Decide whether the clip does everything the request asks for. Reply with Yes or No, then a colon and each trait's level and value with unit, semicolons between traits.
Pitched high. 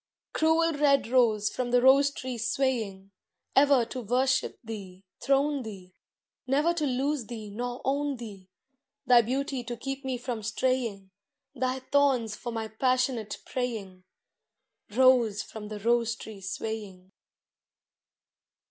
Yes: high, 245 Hz